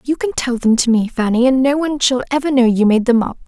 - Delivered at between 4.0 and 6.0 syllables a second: No, 6.3 syllables/s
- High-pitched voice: Yes, very high, 250 Hz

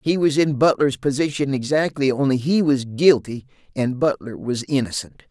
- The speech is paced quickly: No, average, 160 wpm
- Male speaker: Yes, male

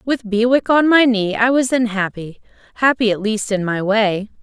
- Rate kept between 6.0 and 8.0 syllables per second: No, 4.7 syllables/s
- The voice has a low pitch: No, high, 225 Hz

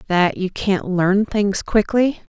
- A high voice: Yes, high, 200 Hz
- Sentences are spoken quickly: No, average, 150 wpm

